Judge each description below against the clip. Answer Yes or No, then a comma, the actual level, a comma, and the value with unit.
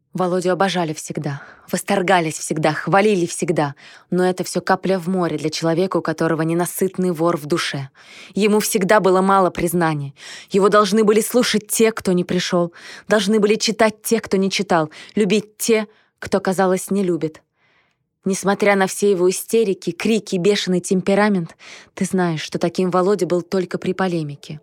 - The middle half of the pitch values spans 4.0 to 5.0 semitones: No, average, 2.8 semitones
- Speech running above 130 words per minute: Yes, average, 155 wpm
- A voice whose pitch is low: No, medium, 185 Hz